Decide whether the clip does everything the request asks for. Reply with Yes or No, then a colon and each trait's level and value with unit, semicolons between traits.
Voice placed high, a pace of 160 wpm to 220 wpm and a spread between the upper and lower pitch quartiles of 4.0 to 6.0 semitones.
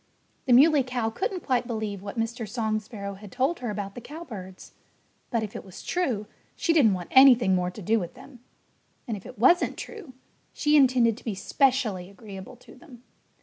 Yes: high, 230 Hz; average, 190 wpm; average, 4.6 semitones